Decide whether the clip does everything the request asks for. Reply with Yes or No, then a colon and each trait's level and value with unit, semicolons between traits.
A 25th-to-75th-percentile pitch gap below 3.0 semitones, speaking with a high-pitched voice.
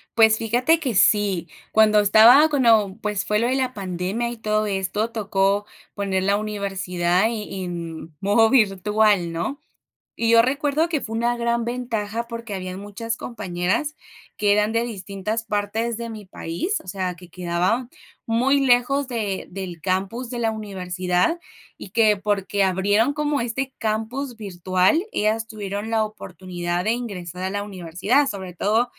No: average, 3.7 semitones; high, 210 Hz